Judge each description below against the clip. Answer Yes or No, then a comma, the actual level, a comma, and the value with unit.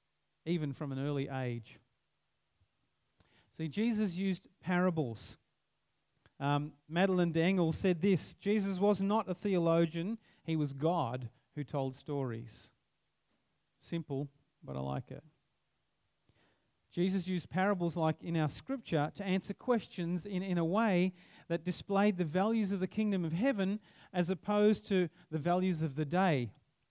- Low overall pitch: No, medium, 170 Hz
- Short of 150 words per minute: Yes, slow, 135 wpm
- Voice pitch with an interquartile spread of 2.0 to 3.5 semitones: No, average, 5.1 semitones